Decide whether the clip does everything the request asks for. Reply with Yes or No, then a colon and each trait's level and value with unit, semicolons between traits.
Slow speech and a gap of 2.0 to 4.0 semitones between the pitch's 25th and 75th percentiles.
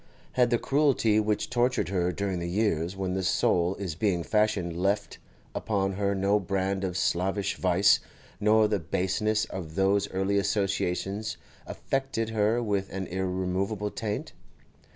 No: average, 145 wpm; narrow, 2.4 semitones